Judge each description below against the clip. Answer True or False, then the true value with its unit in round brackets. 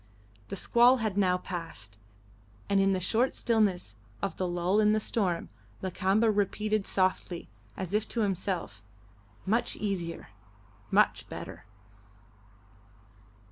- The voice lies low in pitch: False (195 Hz)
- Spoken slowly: True (120 wpm)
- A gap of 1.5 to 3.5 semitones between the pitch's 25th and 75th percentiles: True (3.0 semitones)